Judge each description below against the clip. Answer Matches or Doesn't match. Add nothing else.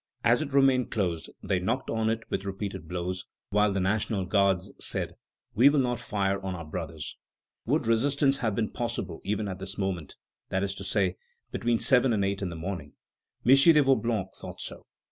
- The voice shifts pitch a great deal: Doesn't match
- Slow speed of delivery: Doesn't match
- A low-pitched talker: Matches